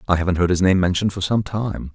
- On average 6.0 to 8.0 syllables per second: Yes, 6.8 syllables/s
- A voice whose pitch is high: No, very low, 95 Hz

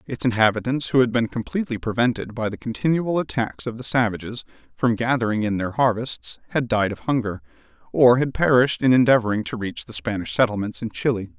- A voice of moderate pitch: No, low, 115 Hz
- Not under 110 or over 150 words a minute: No, average, 185 wpm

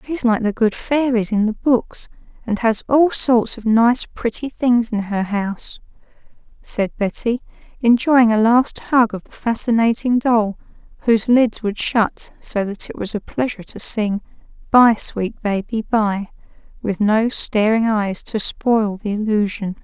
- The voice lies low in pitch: No, high, 225 Hz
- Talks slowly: No, average, 160 wpm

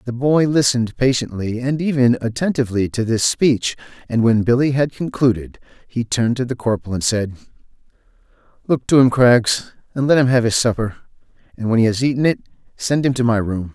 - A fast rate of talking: No, average, 190 wpm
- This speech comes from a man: Yes, male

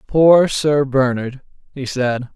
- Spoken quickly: No, slow, 125 wpm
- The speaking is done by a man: Yes, male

